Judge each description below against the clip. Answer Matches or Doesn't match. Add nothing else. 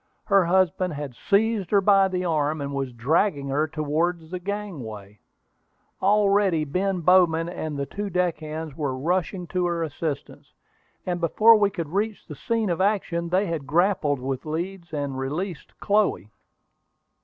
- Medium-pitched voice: Matches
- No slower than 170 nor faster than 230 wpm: Doesn't match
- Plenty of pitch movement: Doesn't match